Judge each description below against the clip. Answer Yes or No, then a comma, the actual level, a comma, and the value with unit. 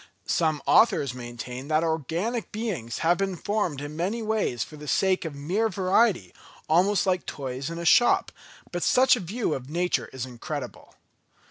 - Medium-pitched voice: Yes, medium, 170 Hz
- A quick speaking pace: No, average, 165 wpm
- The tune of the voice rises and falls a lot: Yes, wide, 6.3 semitones